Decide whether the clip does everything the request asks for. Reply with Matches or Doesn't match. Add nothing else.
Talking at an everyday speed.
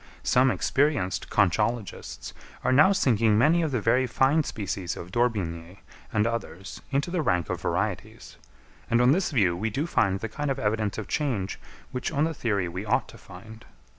Matches